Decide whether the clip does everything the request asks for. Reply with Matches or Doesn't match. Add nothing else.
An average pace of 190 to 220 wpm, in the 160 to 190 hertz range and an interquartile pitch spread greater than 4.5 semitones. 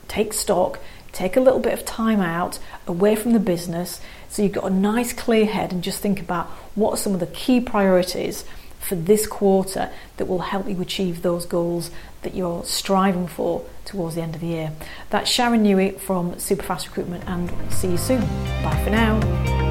Doesn't match